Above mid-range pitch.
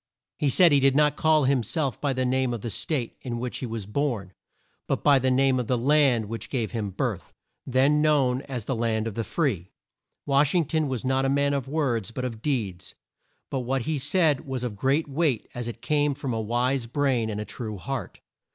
No: low, 130 Hz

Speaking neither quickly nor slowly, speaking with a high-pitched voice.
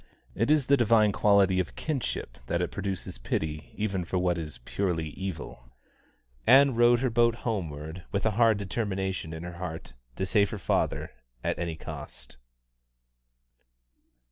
No: average, 150 wpm; very low, 95 Hz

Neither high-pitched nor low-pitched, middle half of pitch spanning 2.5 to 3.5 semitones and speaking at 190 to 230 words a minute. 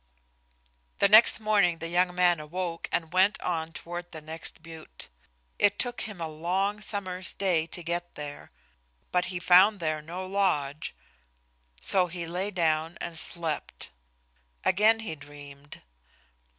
No: medium, 175 Hz; average, 2.9 semitones; average, 140 wpm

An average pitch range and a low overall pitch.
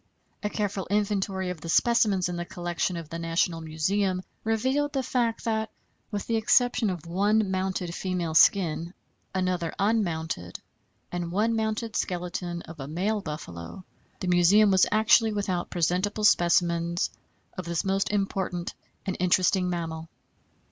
No: average, 3.4 semitones; medium, 185 Hz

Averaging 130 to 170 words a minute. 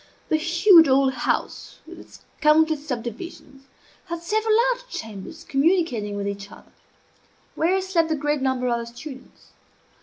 Yes: average, 145 wpm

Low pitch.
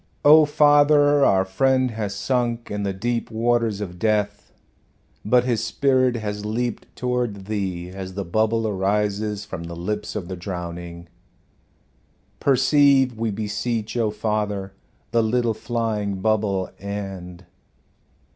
Yes: low, 105 Hz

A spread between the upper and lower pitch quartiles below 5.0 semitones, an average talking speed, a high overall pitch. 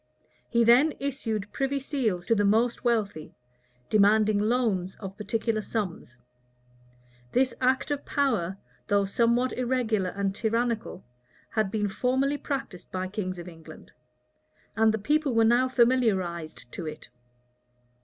No: average, 4.3 semitones; slow, 130 wpm; high, 220 Hz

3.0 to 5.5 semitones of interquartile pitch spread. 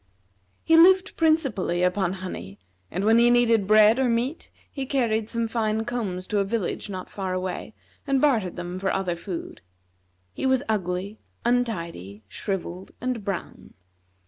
Yes: average, 4.7 semitones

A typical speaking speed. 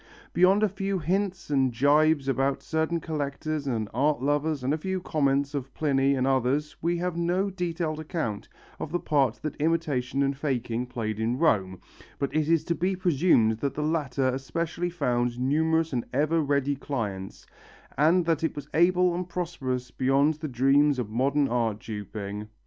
Yes: average, 170 wpm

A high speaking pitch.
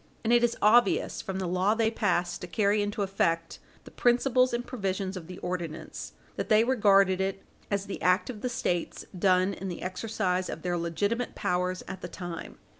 Yes: high, 195 Hz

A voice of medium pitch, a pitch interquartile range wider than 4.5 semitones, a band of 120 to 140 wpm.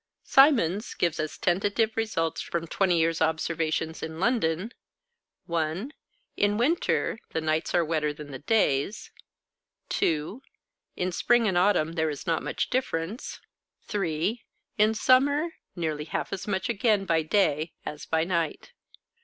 Yes: medium, 170 Hz; average, 5.2 semitones; slow, 135 wpm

